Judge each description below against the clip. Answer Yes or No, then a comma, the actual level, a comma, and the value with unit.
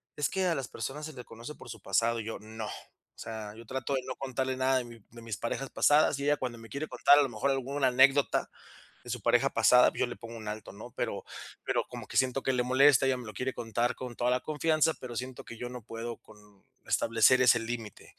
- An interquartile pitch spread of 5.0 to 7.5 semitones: No, average, 2.9 semitones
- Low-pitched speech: Yes, low, 125 Hz